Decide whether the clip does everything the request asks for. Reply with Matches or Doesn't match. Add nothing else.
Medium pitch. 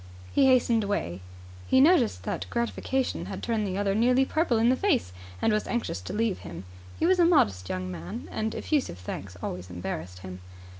Doesn't match